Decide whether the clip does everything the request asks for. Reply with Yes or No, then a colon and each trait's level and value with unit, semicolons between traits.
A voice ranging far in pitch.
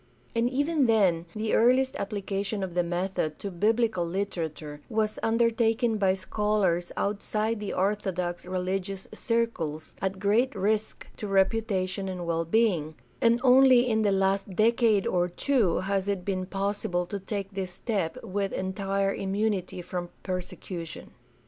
No: average, 3.1 semitones